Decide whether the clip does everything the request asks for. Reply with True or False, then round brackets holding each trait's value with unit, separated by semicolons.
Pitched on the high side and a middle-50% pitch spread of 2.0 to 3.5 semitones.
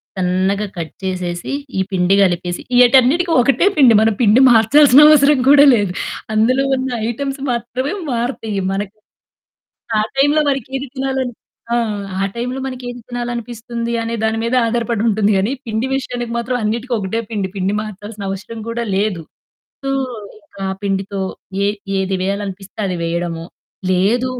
False (225 Hz; 4.3 semitones)